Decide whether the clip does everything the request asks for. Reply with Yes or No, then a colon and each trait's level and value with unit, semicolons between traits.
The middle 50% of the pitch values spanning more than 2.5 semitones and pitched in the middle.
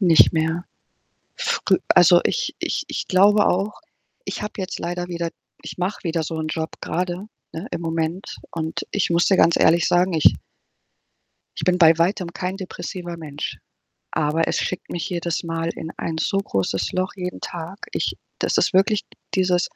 No: narrow, 2.2 semitones; medium, 175 Hz